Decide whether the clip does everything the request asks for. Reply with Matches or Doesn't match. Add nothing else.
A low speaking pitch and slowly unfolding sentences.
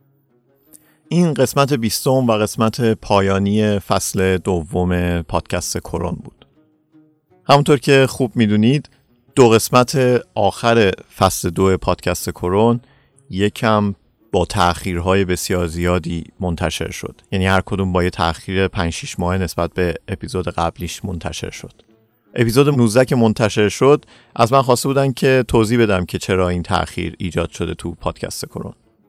Doesn't match